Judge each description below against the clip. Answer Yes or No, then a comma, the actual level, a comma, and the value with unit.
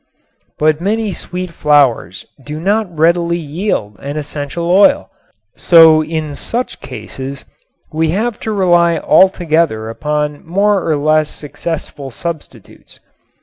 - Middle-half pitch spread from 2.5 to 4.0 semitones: Yes, average, 3.5 semitones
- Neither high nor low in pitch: Yes, medium, 160 Hz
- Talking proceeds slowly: Yes, slow, 115 wpm